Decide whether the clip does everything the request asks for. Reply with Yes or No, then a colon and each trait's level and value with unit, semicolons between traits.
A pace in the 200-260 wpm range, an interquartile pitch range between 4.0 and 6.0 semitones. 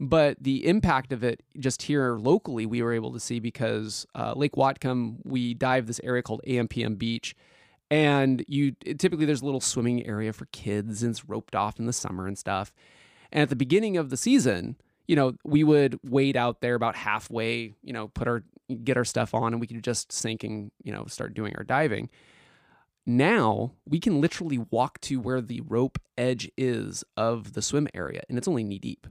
No: fast, 205 wpm; average, 3.2 semitones